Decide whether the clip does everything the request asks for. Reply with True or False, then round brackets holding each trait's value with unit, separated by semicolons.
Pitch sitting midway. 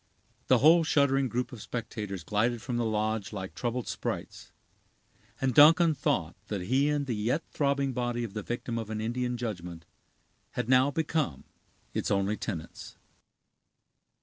False (120 Hz)